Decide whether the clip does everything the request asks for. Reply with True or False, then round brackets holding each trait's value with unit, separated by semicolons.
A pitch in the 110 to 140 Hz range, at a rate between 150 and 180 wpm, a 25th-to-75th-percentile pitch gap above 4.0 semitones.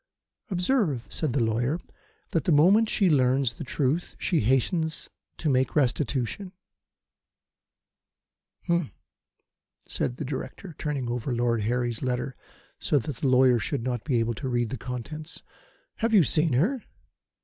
False (135 Hz; 140 wpm; 4.7 semitones)